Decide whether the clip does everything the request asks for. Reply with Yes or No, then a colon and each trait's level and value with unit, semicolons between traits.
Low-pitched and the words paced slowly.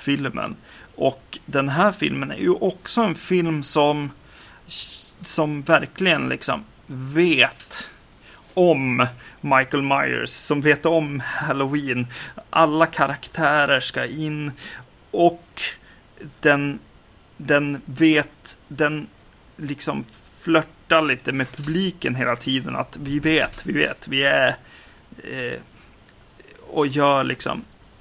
No: medium, 145 Hz; slow, 105 wpm